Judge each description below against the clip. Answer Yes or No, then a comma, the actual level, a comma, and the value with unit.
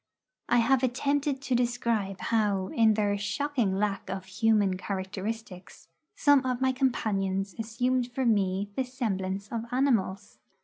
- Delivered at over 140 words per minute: No, slow, 135 wpm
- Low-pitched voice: No, high, 220 Hz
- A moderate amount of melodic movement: Yes, average, 4.4 semitones